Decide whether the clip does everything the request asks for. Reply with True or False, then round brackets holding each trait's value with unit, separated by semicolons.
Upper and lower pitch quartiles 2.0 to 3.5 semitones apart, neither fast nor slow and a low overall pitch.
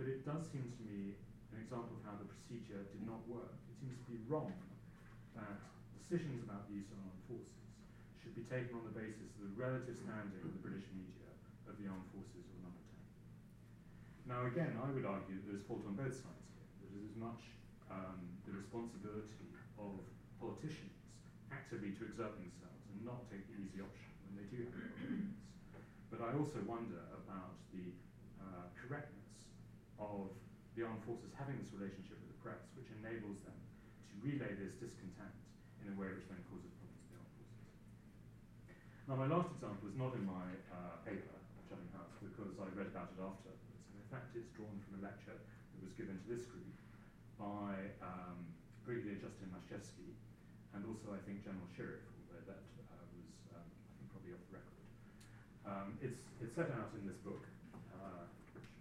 True (3.2 semitones; 185 wpm; 105 Hz)